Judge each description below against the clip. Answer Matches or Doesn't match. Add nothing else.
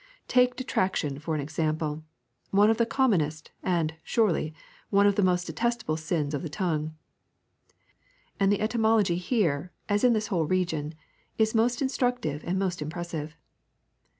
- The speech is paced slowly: Doesn't match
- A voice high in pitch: Doesn't match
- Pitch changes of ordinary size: Doesn't match